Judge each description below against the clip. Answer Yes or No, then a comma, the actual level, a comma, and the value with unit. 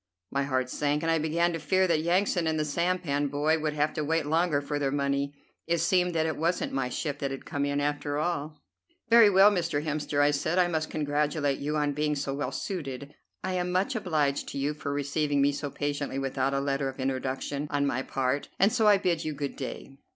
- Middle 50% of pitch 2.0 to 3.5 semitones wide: Yes, average, 2.7 semitones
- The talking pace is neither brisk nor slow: No, fast, 225 wpm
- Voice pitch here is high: No, medium, 150 Hz